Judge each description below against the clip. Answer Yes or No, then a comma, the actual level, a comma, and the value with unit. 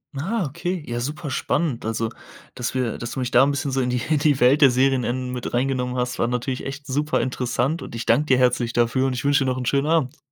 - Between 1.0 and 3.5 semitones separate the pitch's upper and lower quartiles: Yes, narrow, 2.5 semitones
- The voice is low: Yes, low, 130 Hz